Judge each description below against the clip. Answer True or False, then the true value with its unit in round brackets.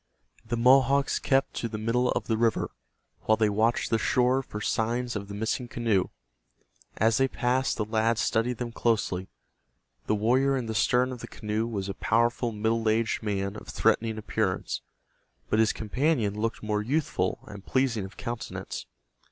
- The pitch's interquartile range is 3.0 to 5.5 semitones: False (2.5 semitones)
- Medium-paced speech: True (170 wpm)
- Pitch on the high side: False (115 Hz)